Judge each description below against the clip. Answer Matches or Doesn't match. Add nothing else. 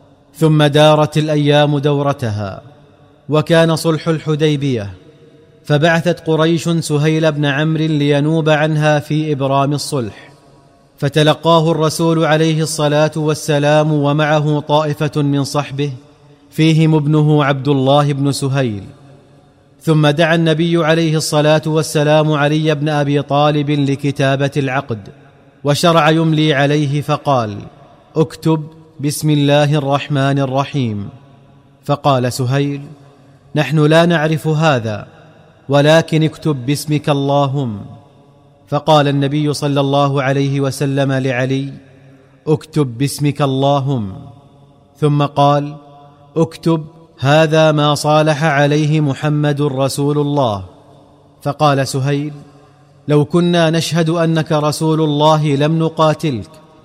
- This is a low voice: Doesn't match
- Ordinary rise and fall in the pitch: Doesn't match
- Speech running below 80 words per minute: Doesn't match